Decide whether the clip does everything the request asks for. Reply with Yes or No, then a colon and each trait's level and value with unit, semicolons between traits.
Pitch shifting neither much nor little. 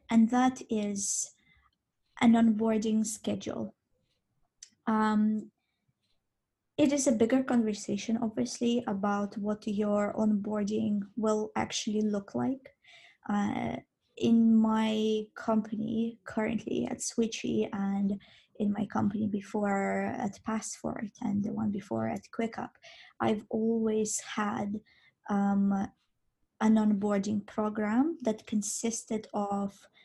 No: narrow, 1.7 semitones